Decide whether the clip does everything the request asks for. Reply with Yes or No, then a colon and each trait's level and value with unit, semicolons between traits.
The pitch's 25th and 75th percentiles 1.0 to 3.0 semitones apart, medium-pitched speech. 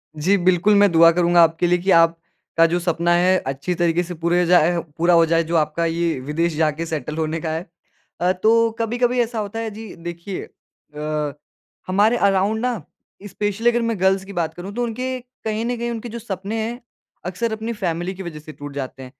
No: average, 4.6 semitones; medium, 175 Hz